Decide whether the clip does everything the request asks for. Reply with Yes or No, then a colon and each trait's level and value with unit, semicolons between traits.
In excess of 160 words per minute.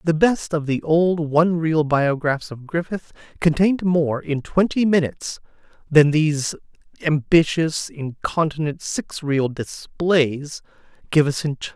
No: average, 140 wpm